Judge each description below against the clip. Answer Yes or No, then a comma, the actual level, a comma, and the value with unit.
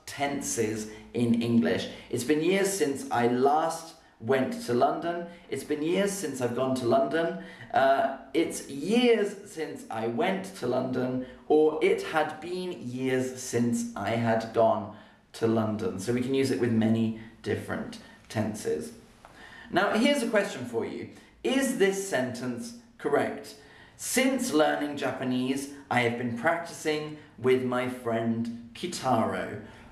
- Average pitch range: No, wide, 6.2 semitones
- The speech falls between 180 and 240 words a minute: No, average, 140 wpm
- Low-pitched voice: Yes, low, 130 Hz